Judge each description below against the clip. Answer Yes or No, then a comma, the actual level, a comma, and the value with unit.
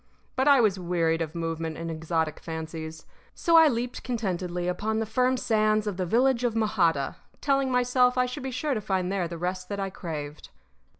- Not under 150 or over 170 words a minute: No, average, 195 wpm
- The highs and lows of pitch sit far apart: Yes, wide, 6.8 semitones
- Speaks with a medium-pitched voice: No, high, 195 Hz